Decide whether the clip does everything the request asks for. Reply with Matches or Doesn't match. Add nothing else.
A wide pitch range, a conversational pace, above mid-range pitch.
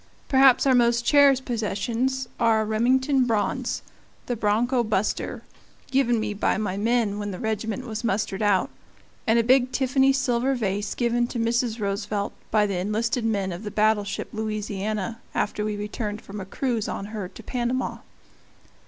Doesn't match